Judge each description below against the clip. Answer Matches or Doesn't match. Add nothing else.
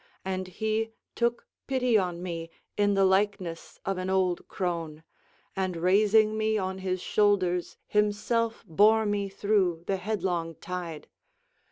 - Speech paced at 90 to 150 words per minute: Matches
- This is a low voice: Doesn't match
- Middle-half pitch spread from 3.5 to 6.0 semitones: Doesn't match